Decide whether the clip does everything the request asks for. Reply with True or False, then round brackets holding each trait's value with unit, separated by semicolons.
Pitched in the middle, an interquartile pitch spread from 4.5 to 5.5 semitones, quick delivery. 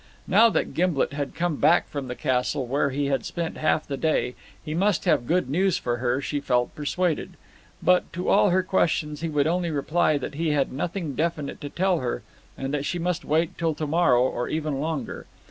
False (155 Hz; 3.8 semitones; 210 wpm)